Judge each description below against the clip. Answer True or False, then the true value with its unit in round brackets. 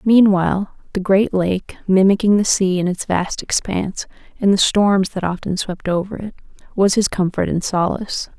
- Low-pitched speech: False (190 Hz)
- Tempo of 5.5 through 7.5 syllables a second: False (4.9 syllables/s)